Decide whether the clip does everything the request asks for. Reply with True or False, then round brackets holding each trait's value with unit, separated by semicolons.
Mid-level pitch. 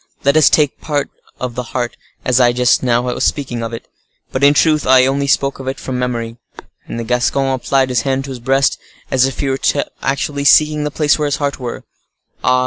False (130 Hz)